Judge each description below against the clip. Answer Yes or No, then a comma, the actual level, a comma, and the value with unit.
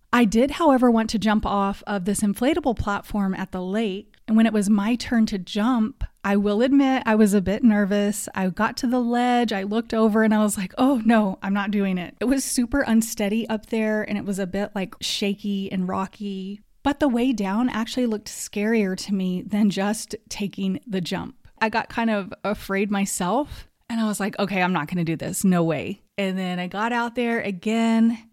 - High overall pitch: Yes, high, 210 Hz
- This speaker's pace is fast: Yes, fast, 215 wpm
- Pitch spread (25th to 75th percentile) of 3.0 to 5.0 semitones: No, narrow, 2.6 semitones